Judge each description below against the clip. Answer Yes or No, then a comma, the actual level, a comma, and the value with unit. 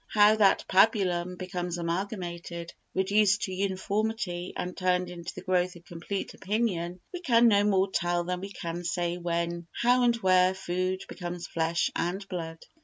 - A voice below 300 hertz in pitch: Yes, medium, 185 Hz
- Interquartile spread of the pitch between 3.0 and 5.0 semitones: No, narrow, 2.4 semitones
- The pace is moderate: Yes, average, 160 wpm